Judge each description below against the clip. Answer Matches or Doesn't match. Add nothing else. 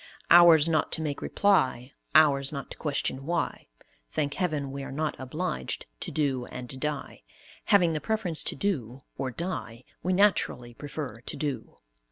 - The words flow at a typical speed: Matches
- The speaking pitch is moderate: Matches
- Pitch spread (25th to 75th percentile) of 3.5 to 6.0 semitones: Matches